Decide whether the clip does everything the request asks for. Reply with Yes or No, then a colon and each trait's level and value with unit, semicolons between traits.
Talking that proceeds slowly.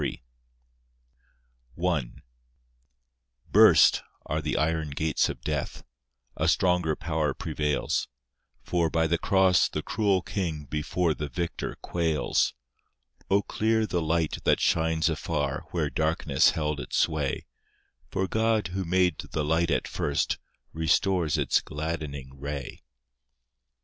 Yes: slow, 120 wpm